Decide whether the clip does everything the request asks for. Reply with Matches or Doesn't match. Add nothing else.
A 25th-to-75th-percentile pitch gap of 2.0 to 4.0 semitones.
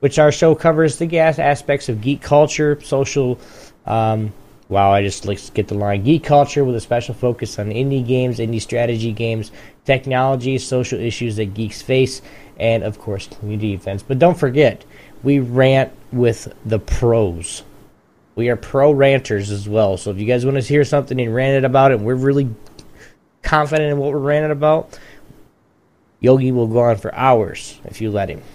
Doesn't match